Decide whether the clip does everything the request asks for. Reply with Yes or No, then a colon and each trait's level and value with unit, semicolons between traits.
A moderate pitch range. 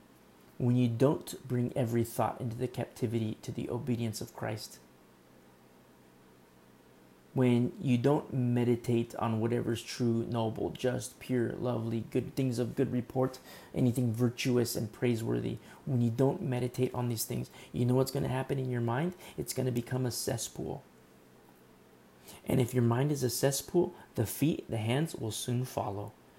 No: narrow, 2.3 semitones